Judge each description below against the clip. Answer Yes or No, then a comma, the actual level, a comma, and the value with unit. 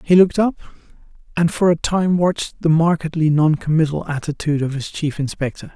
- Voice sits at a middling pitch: Yes, medium, 160 Hz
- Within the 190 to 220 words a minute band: No, average, 175 wpm